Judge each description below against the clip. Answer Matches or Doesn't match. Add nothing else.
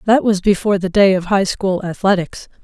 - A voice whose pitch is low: Doesn't match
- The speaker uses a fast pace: Doesn't match